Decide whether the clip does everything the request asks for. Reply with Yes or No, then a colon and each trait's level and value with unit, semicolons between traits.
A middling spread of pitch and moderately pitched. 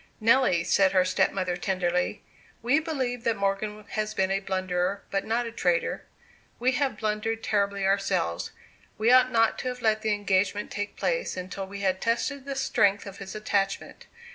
No: average, 3.2 semitones; high, 205 Hz